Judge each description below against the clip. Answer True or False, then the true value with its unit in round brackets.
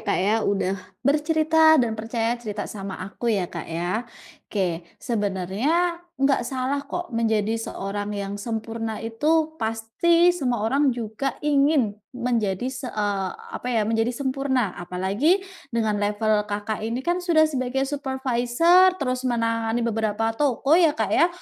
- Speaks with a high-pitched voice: True (230 Hz)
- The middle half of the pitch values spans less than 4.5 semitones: False (4.9 semitones)